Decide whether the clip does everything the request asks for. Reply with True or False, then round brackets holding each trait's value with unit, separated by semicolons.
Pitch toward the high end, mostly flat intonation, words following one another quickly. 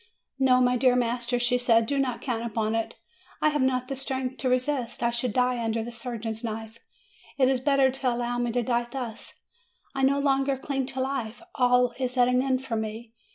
True (250 Hz; 1.9 semitones; 210 wpm)